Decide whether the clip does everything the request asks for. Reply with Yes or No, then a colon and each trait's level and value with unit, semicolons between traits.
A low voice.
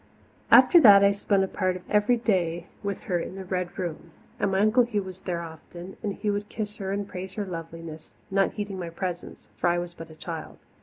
No: high, 190 Hz